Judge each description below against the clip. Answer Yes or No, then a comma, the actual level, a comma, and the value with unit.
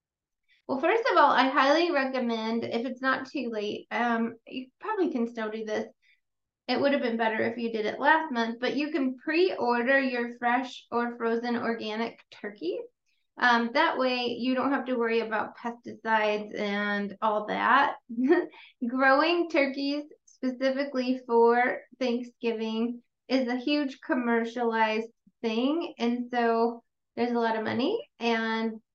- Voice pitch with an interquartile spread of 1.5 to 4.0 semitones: Yes, average, 3.0 semitones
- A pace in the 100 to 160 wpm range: Yes, average, 145 wpm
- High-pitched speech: Yes, high, 245 Hz